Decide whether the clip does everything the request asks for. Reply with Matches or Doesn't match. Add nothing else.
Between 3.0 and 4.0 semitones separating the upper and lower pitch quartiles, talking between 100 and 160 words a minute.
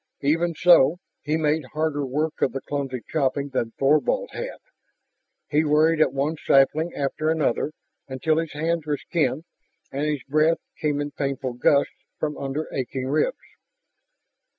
Doesn't match